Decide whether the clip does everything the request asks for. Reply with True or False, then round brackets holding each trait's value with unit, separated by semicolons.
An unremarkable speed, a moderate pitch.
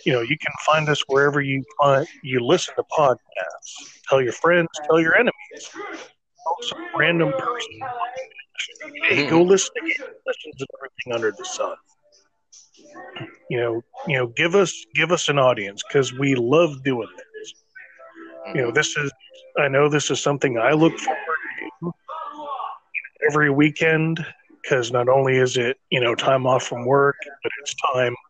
True (165 wpm; 155 Hz)